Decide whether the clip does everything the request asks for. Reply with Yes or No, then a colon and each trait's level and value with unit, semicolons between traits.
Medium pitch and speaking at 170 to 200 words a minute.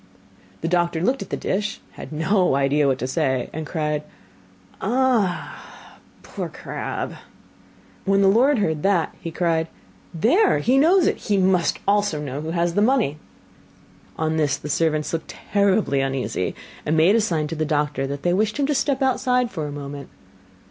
Yes: medium, 170 Hz; average, 175 wpm